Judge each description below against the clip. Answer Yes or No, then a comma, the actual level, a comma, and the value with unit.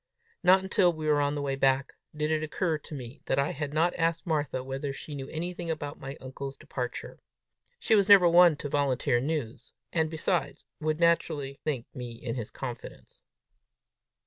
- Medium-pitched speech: Yes, medium, 150 Hz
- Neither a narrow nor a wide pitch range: Yes, average, 3.5 semitones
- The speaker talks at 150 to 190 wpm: Yes, average, 180 wpm